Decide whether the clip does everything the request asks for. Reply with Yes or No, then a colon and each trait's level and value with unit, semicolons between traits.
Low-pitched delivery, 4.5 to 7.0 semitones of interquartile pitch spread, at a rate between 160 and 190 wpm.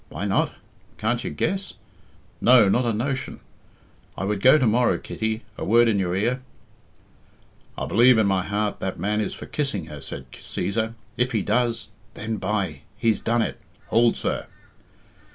No: low, 110 Hz; average, 3.1 semitones; average, 170 wpm